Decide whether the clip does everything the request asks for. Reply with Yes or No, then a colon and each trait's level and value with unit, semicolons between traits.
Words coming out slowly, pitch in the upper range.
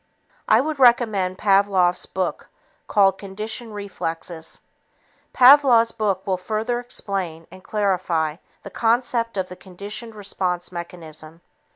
Yes: slow, 110 wpm; high, 195 Hz